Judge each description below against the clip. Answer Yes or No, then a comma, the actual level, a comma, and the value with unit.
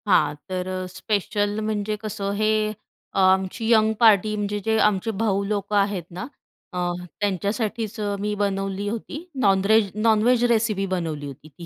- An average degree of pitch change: No, narrow, 2.0 semitones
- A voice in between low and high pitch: No, high, 205 Hz